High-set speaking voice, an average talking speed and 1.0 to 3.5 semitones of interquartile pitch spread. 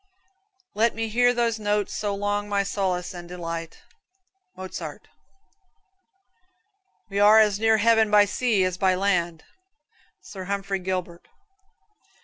No: high, 200 Hz; slow, 125 wpm; narrow, 2.6 semitones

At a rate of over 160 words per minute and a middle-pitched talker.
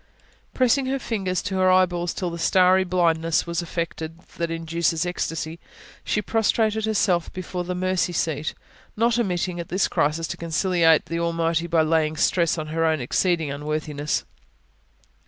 No: average, 155 wpm; medium, 170 Hz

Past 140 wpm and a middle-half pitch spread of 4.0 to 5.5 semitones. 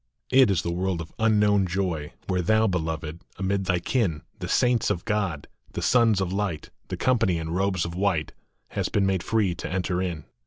No: average, 195 wpm; average, 3.3 semitones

